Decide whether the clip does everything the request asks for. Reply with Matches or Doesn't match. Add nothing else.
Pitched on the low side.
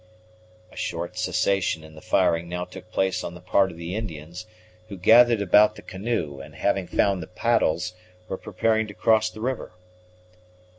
Matches